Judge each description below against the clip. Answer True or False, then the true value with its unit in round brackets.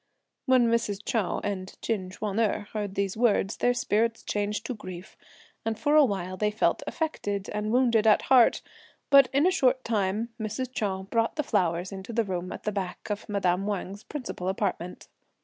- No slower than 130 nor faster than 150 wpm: False (185 wpm)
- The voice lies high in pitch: True (210 Hz)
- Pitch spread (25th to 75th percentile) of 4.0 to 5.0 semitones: False (3.3 semitones)